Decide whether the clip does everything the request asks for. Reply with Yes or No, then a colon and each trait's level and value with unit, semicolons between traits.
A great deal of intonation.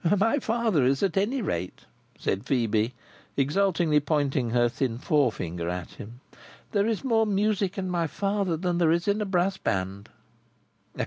Yes: wide, 8.7 semitones